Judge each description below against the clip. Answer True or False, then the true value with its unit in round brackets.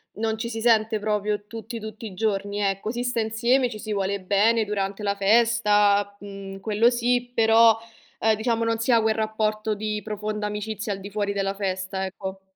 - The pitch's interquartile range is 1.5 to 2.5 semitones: True (1.9 semitones)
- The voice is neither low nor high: False (215 Hz)